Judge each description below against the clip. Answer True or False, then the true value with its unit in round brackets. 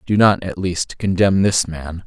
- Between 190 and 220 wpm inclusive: True (205 wpm)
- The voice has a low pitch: True (95 Hz)